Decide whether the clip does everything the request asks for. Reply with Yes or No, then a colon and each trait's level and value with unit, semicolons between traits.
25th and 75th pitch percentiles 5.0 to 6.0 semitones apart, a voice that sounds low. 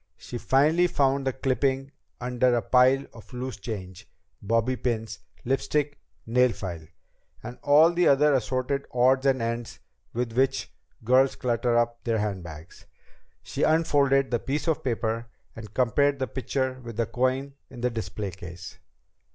No: average, 2.9 semitones; low, 125 Hz